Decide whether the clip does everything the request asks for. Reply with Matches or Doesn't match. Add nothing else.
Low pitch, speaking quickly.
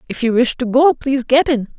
Doesn't match